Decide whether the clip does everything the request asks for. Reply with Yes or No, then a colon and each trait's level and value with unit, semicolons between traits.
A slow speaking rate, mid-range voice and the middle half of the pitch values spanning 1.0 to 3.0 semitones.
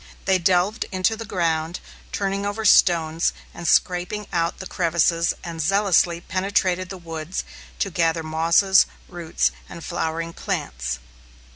Yes: slow, 130 wpm; medium, 175 Hz; narrow, 2.6 semitones